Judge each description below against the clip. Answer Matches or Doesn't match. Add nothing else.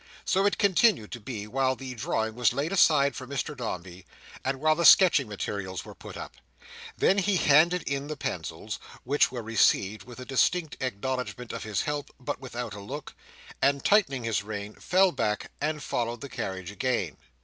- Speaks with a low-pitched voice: Matches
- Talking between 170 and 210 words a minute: Matches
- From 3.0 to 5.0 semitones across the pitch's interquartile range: Doesn't match